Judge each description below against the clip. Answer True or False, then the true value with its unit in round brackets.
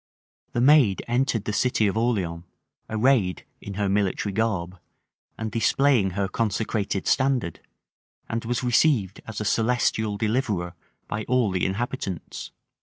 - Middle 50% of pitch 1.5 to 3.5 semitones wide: False (3.9 semitones)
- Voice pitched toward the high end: False (110 Hz)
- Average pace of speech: False (130 wpm)